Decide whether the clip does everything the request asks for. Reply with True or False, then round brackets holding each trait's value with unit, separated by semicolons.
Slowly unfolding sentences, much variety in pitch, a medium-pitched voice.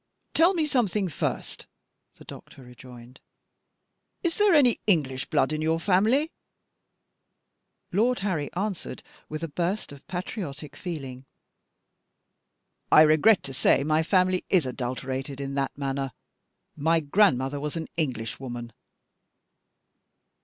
True (115 wpm; 6.2 semitones; 155 Hz)